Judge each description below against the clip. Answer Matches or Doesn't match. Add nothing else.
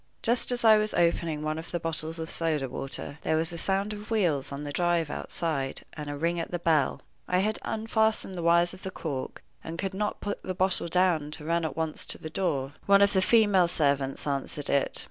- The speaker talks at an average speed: Doesn't match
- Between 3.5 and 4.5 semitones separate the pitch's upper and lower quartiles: Matches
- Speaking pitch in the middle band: Matches